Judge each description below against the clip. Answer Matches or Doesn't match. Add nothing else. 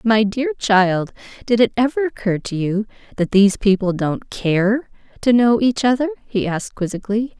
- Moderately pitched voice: Doesn't match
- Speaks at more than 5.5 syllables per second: Doesn't match